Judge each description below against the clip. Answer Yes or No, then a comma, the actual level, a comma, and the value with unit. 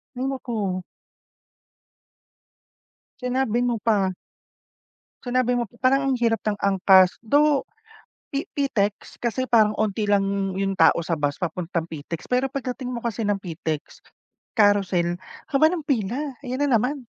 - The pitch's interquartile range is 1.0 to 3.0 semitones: No, average, 4.8 semitones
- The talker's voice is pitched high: Yes, high, 220 Hz